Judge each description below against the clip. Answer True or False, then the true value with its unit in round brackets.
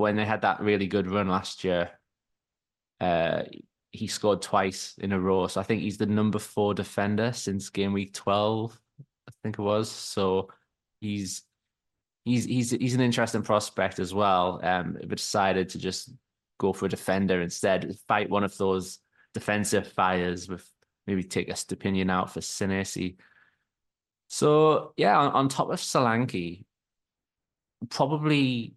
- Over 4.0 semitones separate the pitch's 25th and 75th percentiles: False (3.3 semitones)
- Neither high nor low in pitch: False (105 Hz)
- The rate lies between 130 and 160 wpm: True (155 wpm)